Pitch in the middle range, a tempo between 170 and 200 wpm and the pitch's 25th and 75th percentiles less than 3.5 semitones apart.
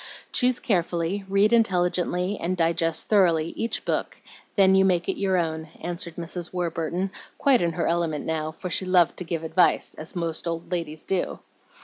Yes: medium, 175 Hz; average, 175 wpm; narrow, 2.4 semitones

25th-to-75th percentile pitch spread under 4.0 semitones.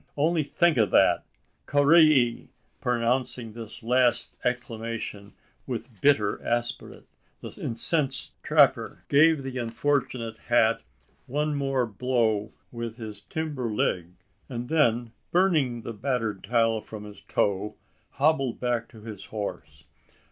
Yes: average, 3.5 semitones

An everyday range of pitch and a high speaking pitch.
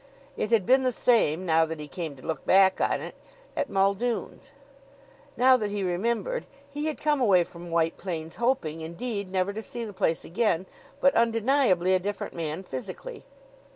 No: wide, 5.9 semitones; high, 195 Hz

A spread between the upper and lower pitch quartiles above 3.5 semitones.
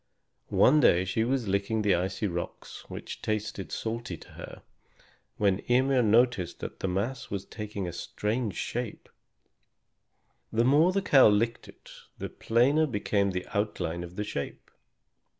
Yes: average, 4.1 semitones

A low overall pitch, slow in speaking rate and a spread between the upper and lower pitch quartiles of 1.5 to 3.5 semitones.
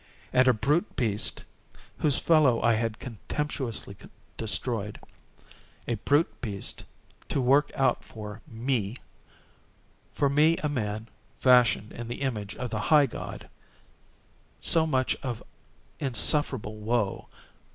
No: low, 125 Hz; slow, 110 wpm; average, 4.3 semitones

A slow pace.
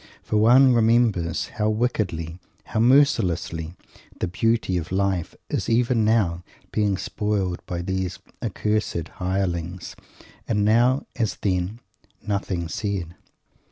Yes: slow, 115 wpm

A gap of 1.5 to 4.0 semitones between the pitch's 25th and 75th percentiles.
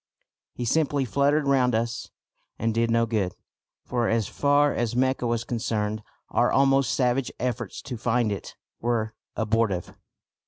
Yes: average, 2.7 semitones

